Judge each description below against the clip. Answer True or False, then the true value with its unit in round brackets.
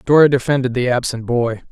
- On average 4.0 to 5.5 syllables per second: False (5.9 syllables/s)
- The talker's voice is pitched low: True (125 Hz)